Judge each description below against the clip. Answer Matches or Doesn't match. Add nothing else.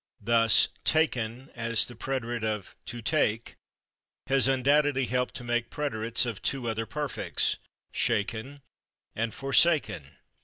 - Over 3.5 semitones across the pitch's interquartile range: Doesn't match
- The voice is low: Matches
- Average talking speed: Doesn't match